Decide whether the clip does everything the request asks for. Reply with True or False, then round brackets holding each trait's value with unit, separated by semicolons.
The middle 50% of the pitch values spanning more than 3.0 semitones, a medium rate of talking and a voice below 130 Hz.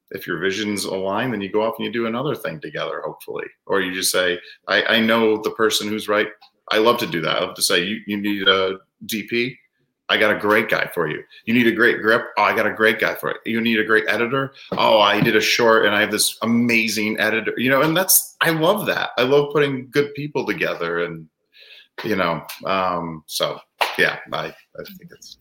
False (4.7 semitones; 235 wpm; 115 Hz)